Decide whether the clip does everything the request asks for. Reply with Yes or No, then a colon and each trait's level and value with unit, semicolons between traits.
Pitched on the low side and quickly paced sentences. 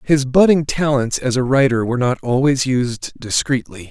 No: low, 130 Hz; average, 170 wpm